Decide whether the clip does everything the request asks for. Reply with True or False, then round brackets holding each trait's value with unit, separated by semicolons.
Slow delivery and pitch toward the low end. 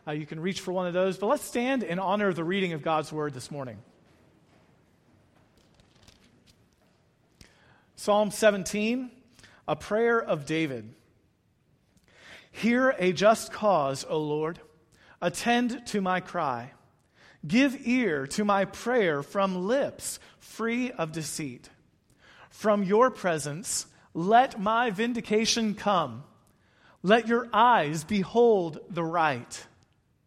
False (120 wpm; 190 Hz)